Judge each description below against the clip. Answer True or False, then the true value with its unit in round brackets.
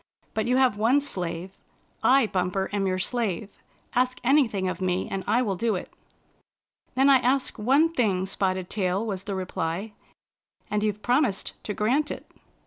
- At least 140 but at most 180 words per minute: True (175 wpm)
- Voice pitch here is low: False (210 Hz)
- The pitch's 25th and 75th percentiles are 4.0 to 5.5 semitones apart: True (5.0 semitones)